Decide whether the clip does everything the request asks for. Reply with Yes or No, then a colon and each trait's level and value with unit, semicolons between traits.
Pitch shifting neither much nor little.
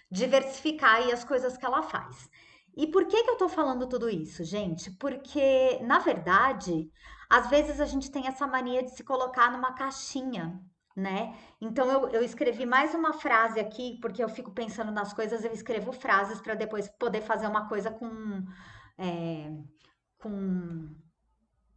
Yes: average, 4.3 semitones